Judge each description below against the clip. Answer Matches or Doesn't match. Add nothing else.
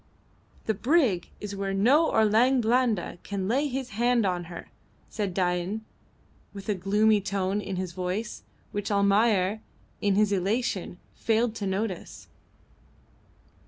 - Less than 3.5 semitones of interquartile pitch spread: Matches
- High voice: Matches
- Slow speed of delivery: Matches